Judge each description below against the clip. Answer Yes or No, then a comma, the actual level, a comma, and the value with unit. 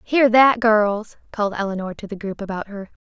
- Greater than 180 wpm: Yes, average, 200 wpm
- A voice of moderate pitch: No, high, 210 Hz